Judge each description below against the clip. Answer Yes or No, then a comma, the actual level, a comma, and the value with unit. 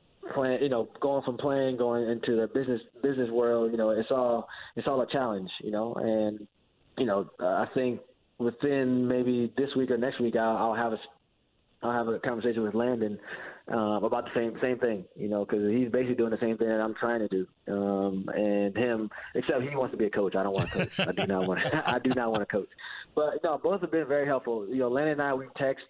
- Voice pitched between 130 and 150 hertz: No, low, 120 Hz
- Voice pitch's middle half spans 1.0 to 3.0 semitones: Yes, average, 2.7 semitones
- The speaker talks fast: Yes, fast, 245 wpm